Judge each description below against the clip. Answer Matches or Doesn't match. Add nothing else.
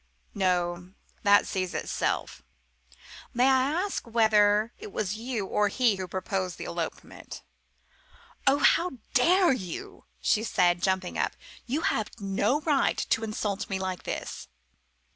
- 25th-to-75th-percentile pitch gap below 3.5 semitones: Doesn't match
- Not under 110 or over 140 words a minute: Matches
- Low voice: Doesn't match